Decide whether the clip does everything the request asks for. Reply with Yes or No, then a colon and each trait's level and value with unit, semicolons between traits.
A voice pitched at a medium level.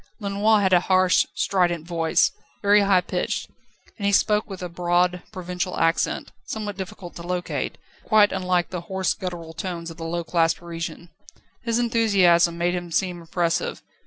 Yes: medium, 180 Hz